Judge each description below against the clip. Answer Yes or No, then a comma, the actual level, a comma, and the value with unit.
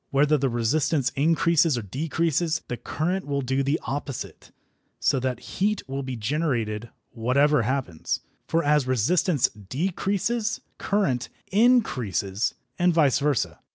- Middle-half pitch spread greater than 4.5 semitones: Yes, average, 5.1 semitones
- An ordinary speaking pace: No, slow, 125 wpm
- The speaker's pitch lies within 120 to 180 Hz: Yes, medium, 140 Hz